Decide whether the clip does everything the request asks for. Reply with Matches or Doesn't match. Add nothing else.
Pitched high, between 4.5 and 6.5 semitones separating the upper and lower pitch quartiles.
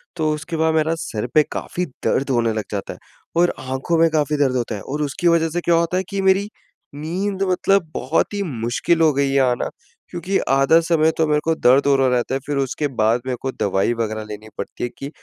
Doesn't match